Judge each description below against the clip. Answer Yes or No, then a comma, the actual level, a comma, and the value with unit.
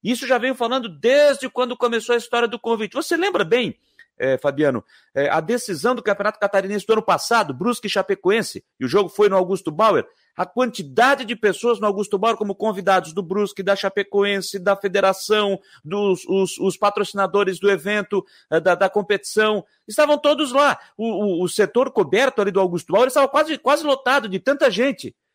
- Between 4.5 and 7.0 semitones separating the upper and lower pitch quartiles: No, average, 4.1 semitones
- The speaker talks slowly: No, fast, 185 wpm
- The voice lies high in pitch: Yes, high, 210 Hz